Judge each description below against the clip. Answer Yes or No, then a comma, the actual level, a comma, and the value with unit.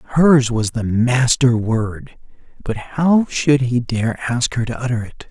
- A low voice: Yes, low, 125 Hz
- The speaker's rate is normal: Yes, average, 170 wpm